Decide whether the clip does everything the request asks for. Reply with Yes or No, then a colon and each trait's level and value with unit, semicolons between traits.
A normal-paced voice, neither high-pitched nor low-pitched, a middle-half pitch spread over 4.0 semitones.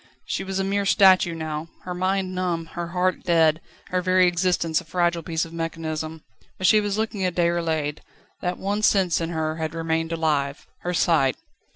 No: average, 185 wpm; medium, 170 Hz; narrow, 2.4 semitones